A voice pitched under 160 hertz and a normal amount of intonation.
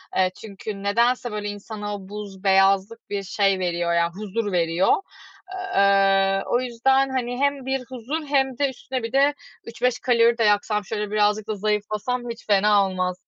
No: high, 210 Hz; average, 3.7 semitones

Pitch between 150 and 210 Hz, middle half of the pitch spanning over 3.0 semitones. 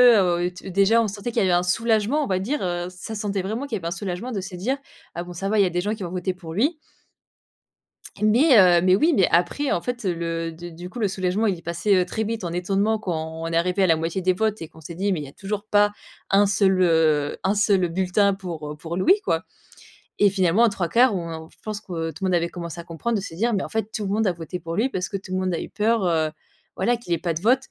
Yes: medium, 185 Hz; average, 3.6 semitones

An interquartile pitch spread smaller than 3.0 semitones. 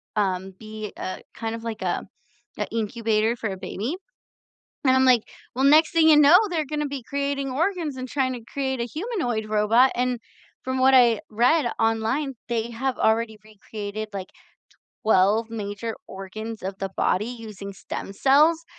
No: average, 4.0 semitones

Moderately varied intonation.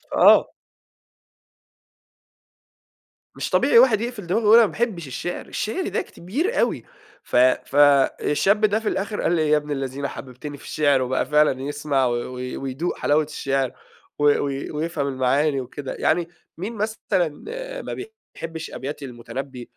No: wide, 7.2 semitones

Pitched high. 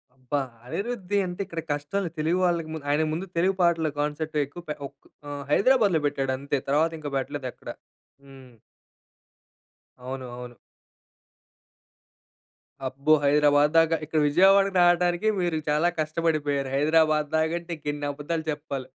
No: medium, 155 Hz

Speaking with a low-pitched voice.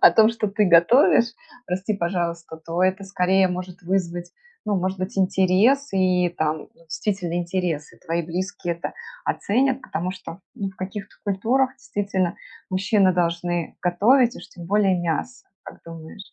No: medium, 185 Hz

